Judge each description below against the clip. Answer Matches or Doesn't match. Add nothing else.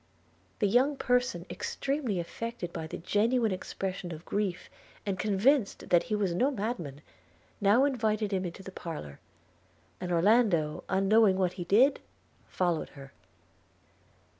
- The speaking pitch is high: Matches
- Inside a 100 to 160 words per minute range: Matches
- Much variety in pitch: Doesn't match